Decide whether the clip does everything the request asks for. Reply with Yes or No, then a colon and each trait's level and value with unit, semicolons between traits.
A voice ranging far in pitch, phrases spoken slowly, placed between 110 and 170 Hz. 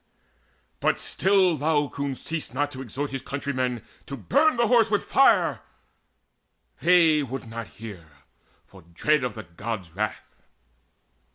Yes: wide, 6.1 semitones; slow, 130 wpm; medium, 140 Hz